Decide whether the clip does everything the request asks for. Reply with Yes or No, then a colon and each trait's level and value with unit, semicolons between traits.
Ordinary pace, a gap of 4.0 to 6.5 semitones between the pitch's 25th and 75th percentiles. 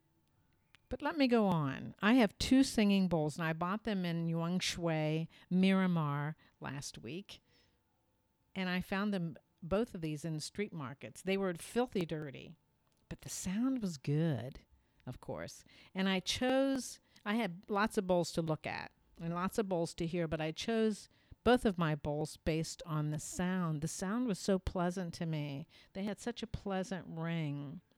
Yes: average, 175 wpm; average, 4.4 semitones